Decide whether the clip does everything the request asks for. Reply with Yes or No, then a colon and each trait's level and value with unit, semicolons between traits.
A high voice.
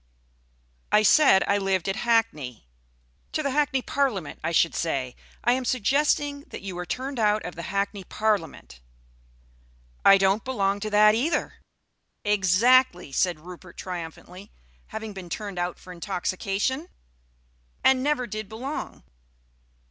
Yes: high, 200 Hz